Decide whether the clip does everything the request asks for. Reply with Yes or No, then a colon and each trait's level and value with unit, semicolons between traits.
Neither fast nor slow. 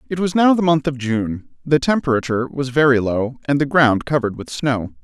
No: fast, 215 wpm